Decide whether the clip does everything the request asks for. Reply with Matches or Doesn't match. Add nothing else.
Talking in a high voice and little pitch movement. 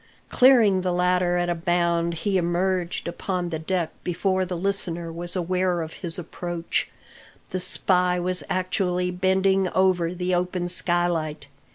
Doesn't match